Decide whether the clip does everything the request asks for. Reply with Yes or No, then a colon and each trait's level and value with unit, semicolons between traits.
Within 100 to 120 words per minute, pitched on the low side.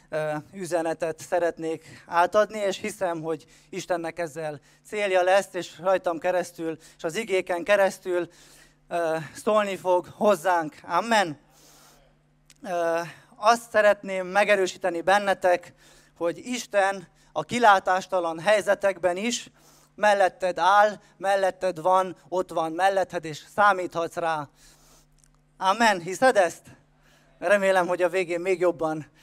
No: slow, 105 wpm; medium, 180 Hz